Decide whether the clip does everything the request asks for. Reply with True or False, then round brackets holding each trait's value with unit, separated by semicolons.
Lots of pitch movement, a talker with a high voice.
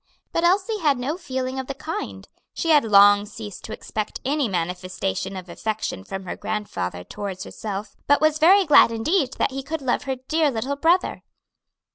True (7.1 semitones; 255 Hz)